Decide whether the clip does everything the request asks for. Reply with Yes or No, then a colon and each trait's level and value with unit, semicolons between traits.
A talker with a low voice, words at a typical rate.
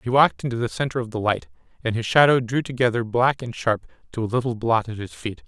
No: low, 120 Hz; fast, 250 wpm